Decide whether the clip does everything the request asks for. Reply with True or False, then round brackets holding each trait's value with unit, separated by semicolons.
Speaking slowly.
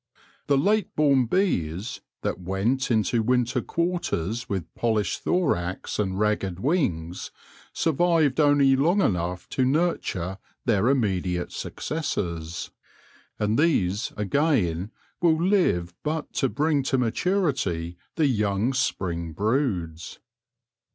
True (110 wpm)